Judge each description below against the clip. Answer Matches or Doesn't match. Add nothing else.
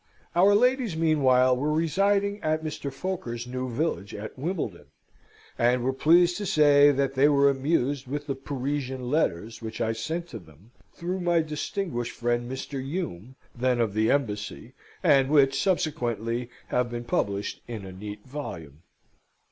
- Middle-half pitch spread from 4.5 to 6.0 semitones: Matches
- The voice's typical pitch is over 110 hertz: Matches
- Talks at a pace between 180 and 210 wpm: Doesn't match